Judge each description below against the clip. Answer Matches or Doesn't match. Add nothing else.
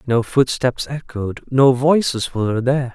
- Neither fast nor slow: Matches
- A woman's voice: Doesn't match